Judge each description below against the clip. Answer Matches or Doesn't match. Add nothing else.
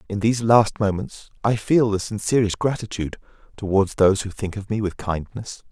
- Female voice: Doesn't match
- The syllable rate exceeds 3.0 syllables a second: Matches